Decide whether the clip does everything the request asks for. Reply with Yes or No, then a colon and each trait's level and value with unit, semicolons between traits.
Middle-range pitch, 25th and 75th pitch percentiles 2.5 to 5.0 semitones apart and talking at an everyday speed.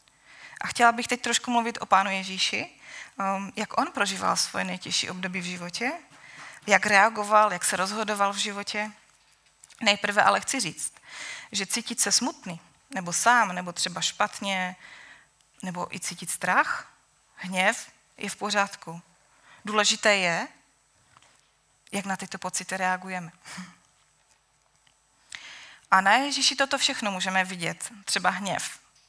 No: high, 200 Hz; average, 2.8 semitones; average, 125 wpm